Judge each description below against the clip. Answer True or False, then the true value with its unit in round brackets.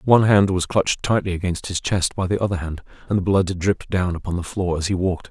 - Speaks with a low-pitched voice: True (95 Hz)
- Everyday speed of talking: False (250 wpm)